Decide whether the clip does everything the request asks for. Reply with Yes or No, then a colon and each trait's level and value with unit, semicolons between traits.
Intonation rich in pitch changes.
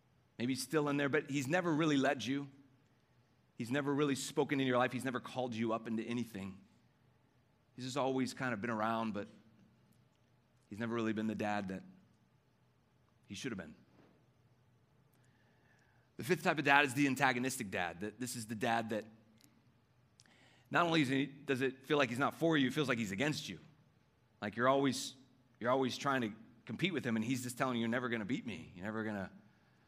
No: average, 2.8 semitones